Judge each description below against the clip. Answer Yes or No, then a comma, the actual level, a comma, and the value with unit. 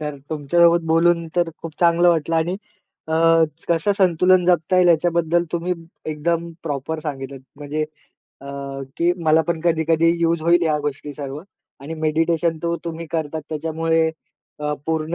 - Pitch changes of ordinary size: No, narrow, 1.8 semitones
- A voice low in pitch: No, medium, 165 Hz